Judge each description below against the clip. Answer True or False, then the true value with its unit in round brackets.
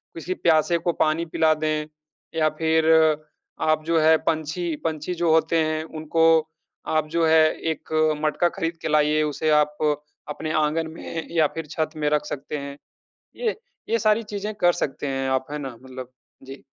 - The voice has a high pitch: False (155 Hz)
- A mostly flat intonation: True (1.6 semitones)